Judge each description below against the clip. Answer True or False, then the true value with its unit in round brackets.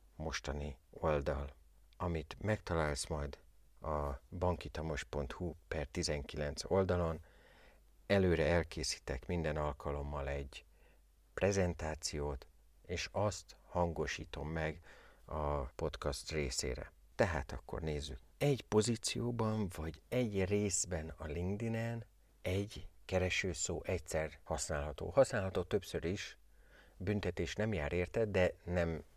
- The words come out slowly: True (95 wpm)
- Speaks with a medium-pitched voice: False (80 Hz)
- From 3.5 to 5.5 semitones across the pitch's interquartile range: True (4.2 semitones)